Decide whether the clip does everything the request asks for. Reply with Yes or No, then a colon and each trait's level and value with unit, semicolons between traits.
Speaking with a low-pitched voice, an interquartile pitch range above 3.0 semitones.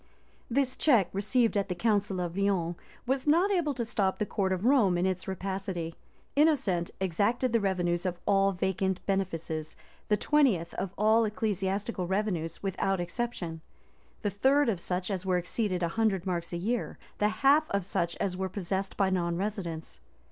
No: high, 195 Hz; average, 3.8 semitones